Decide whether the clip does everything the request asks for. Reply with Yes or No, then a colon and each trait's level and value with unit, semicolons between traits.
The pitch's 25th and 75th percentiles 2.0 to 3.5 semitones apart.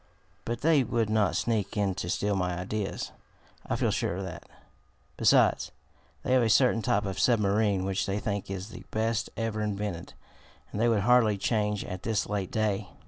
Yes: narrow, 2.5 semitones